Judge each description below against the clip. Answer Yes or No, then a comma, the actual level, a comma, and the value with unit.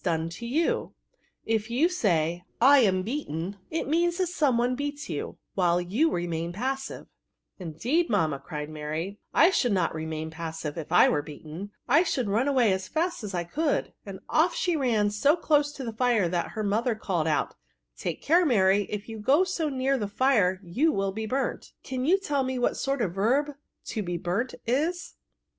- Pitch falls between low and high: No, high, 220 Hz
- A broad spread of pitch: Yes, wide, 8.0 semitones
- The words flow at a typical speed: No, fast, 210 wpm